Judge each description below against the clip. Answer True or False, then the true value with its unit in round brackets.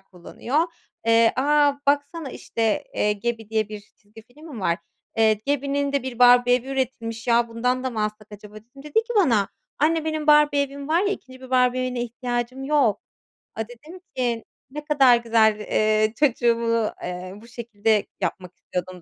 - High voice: True (240 Hz)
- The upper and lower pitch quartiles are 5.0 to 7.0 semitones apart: False (4.3 semitones)